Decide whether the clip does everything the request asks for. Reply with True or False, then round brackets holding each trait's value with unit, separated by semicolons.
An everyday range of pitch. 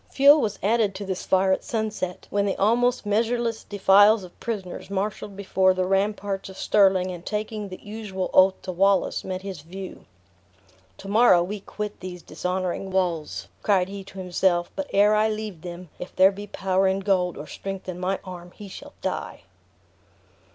False (2.2 semitones)